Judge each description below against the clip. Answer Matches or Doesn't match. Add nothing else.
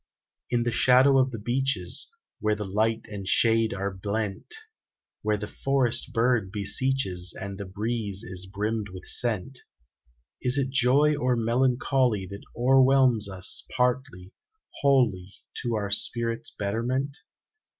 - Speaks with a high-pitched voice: Doesn't match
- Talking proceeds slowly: Matches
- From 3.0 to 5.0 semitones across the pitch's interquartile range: Matches